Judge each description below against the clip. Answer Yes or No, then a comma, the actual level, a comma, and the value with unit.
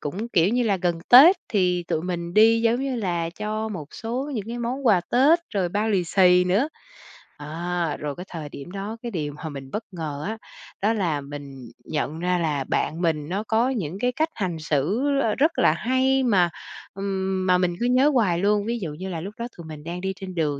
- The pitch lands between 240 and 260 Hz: No, medium, 185 Hz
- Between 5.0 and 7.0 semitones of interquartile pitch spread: Yes, wide, 5.5 semitones